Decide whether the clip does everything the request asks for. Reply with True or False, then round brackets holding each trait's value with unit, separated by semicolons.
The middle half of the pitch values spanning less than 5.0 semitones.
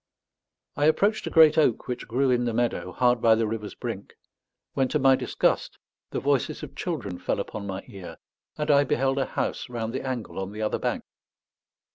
True (4.2 semitones)